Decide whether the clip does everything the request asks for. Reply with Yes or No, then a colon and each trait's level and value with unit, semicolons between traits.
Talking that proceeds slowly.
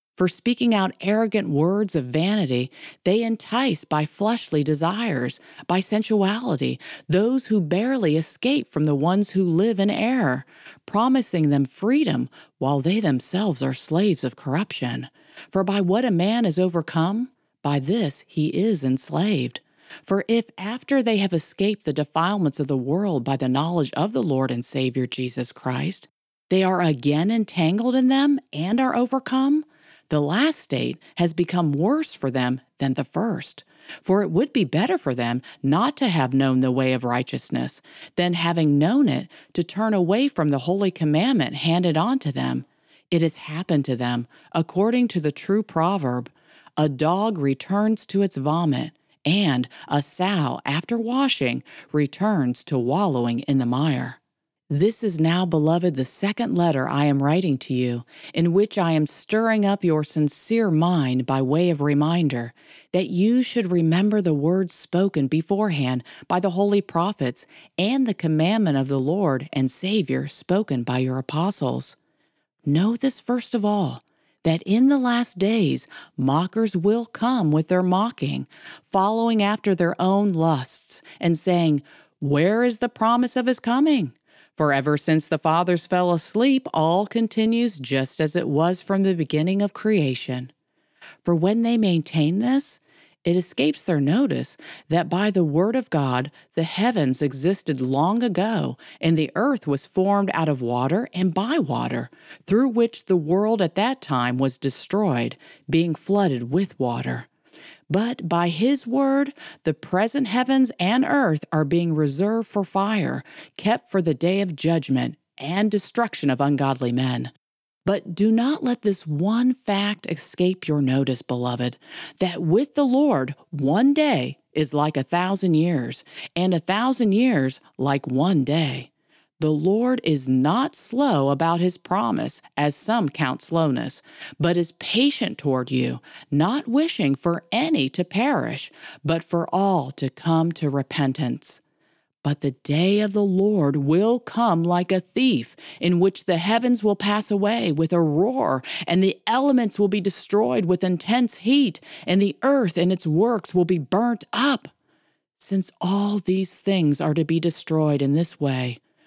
No: average, 160 wpm